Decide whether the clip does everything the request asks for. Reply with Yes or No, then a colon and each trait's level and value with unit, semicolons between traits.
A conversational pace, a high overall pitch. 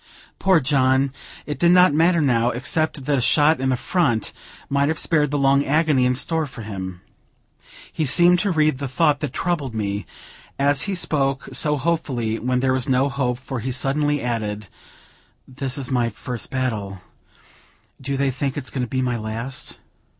No: average, 180 wpm; low, 135 Hz